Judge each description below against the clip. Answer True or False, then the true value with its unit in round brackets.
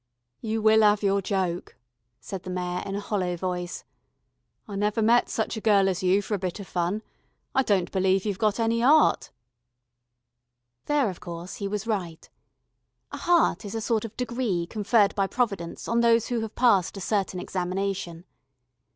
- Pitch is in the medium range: False (200 Hz)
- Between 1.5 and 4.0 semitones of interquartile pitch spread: True (3.3 semitones)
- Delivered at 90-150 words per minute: False (175 wpm)